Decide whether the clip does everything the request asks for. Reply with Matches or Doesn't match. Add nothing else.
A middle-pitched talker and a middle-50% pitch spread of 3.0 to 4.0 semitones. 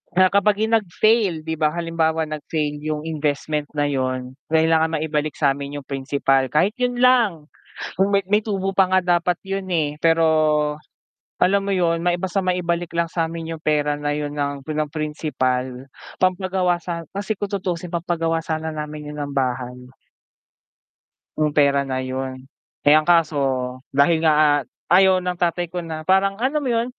Matches